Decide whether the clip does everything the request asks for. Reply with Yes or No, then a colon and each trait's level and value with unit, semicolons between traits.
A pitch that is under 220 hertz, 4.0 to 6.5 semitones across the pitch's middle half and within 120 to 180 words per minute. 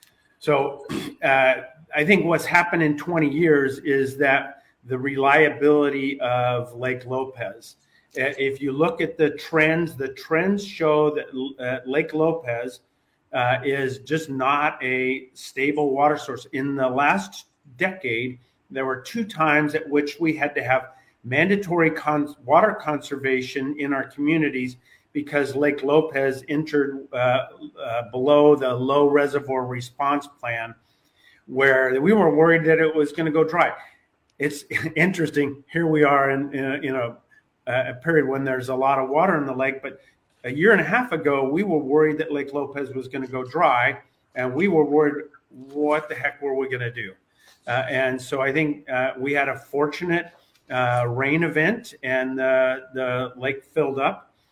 No: medium, 140 Hz; average, 2.9 semitones; average, 165 wpm